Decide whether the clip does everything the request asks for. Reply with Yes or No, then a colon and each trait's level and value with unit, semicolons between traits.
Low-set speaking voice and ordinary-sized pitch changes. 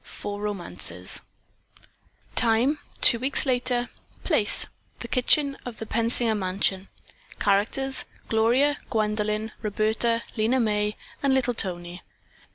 No: high, 220 Hz; average, 3.1 semitones